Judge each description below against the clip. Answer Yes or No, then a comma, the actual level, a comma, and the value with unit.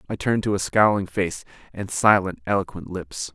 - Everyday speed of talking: Yes, average, 180 wpm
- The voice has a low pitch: Yes, very low, 95 Hz